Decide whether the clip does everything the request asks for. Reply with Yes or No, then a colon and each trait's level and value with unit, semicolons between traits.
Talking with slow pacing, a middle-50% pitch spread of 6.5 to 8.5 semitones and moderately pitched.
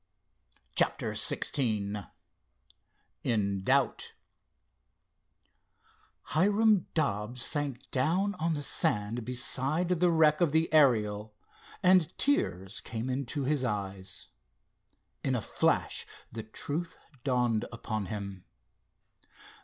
No: slow, 95 wpm; wide, 7.0 semitones; low, 125 Hz